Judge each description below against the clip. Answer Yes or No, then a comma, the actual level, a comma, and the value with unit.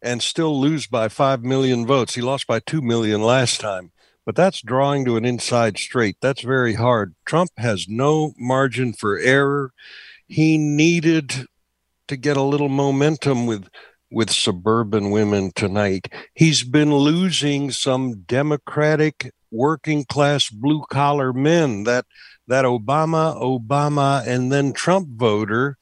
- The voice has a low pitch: Yes, low, 130 Hz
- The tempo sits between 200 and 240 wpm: No, average, 140 wpm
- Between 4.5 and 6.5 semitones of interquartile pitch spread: No, average, 3.8 semitones